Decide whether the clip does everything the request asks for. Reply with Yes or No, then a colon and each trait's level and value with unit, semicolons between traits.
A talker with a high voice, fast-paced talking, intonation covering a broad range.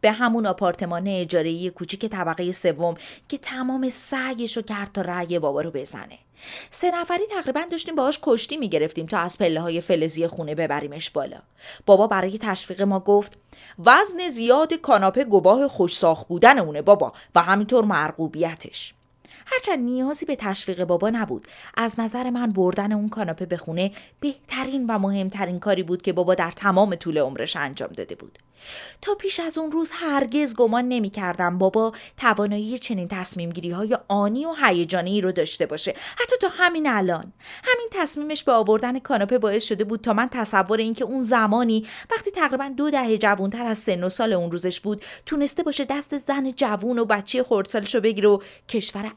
Yes: high, 215 Hz; fast, 170 wpm; wide, 6.1 semitones